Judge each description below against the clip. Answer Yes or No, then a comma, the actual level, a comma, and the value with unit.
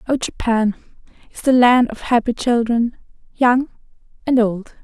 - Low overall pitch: No, high, 240 Hz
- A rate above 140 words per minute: No, slow, 135 wpm